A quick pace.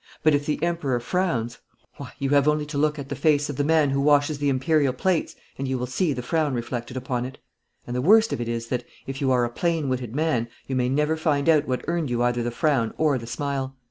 Yes: fast, 255 wpm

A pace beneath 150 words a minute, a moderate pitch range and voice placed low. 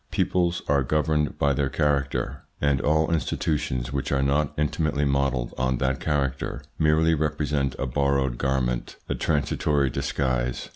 No: average, 140 wpm; narrow, 2.2 semitones; very low, 70 Hz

